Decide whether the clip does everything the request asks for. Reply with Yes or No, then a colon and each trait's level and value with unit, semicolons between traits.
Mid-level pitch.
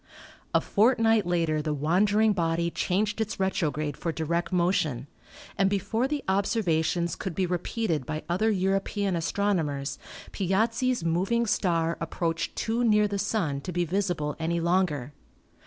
Yes: medium, 180 Hz